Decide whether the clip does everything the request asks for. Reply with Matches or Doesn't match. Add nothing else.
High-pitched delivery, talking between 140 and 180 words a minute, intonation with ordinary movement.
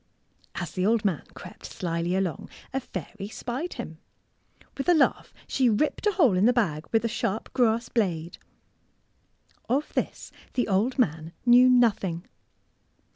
Doesn't match